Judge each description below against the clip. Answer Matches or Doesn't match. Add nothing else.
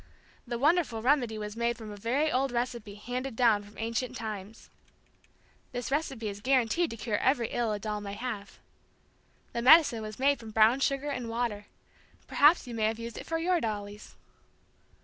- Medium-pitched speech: Doesn't match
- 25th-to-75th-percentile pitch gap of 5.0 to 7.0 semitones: Doesn't match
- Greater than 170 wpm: Matches